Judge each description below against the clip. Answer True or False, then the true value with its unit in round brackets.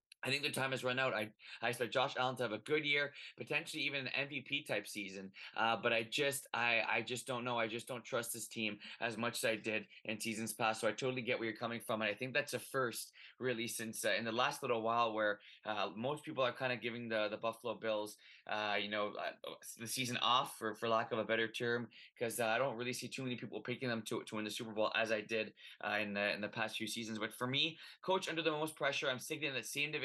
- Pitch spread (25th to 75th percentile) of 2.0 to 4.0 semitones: True (3.0 semitones)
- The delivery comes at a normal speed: False (270 wpm)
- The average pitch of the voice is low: True (115 Hz)